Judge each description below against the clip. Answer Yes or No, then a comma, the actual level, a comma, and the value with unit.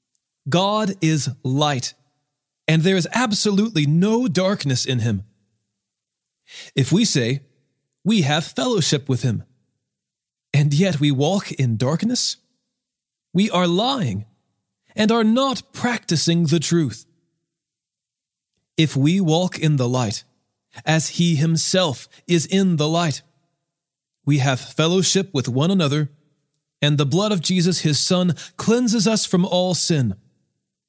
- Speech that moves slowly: Yes, slow, 125 wpm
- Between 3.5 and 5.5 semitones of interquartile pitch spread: Yes, average, 5.1 semitones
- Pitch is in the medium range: Yes, medium, 160 Hz